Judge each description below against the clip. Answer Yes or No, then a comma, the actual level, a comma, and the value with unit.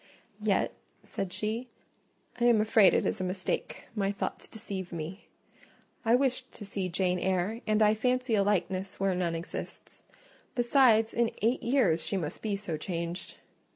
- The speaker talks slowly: No, average, 160 wpm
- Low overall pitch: No, high, 205 Hz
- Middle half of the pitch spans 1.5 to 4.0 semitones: Yes, average, 3.7 semitones